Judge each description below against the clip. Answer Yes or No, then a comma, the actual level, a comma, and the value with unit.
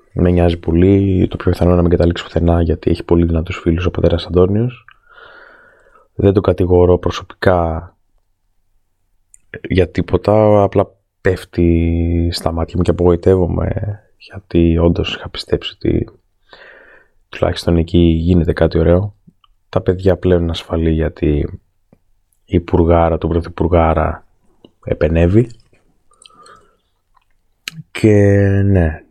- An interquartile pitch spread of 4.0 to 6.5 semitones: No, average, 2.7 semitones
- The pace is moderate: No, slow, 110 wpm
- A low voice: Yes, very low, 90 Hz